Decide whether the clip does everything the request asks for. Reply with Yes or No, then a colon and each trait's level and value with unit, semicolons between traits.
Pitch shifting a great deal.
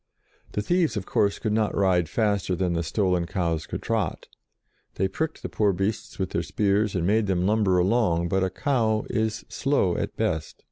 No: average, 3.3 semitones